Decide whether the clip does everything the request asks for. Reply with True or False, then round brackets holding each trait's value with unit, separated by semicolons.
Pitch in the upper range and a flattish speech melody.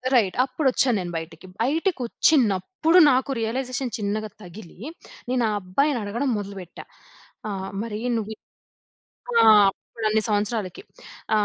False (220 Hz; 4.4 semitones)